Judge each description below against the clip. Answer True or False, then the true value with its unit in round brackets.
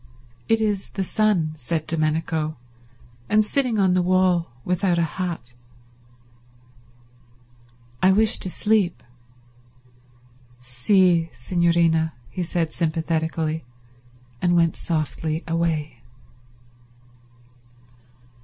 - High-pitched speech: False (170 Hz)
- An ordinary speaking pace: False (90 wpm)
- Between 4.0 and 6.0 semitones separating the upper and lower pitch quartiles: False (2.7 semitones)